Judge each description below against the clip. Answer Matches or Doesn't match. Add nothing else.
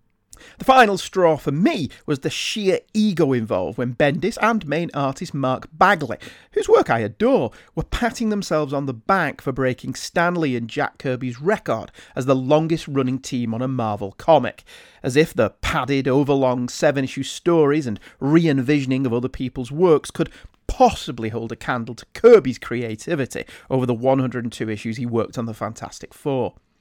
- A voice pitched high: Doesn't match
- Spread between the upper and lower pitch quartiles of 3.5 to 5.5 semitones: Matches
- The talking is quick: Doesn't match